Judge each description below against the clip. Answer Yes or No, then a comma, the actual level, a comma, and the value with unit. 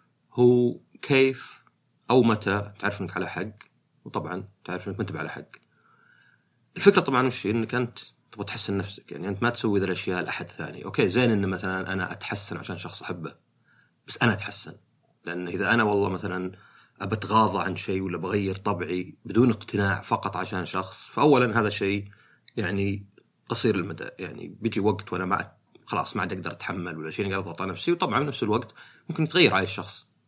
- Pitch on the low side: Yes, low, 100 Hz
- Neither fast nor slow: No, fast, 170 wpm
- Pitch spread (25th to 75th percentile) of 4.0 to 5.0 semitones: No, average, 3.6 semitones